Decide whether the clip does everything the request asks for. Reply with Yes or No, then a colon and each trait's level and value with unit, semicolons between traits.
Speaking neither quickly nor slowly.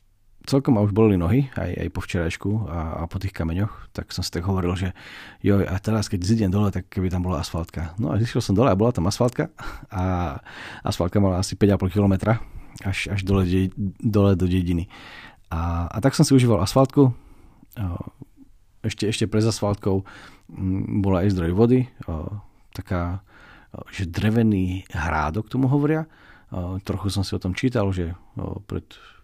No: fast, 175 wpm